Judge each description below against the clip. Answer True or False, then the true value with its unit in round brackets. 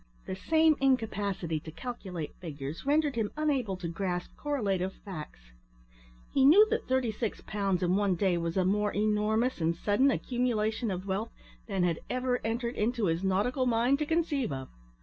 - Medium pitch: False (210 Hz)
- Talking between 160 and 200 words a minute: True (170 wpm)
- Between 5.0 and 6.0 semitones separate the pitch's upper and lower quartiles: True (5.5 semitones)